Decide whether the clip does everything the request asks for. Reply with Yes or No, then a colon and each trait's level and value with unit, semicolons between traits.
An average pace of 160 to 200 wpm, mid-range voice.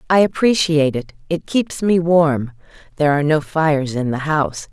Yes: average, 165 wpm; medium, 155 Hz